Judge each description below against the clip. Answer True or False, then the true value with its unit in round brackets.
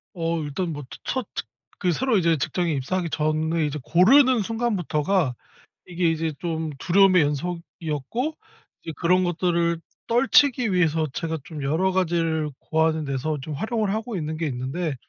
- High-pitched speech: False (170 Hz)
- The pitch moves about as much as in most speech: True (3.3 semitones)